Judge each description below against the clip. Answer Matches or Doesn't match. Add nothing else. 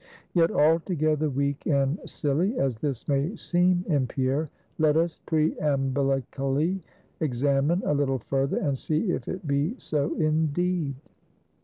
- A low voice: Doesn't match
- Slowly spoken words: Matches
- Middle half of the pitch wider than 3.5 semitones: Doesn't match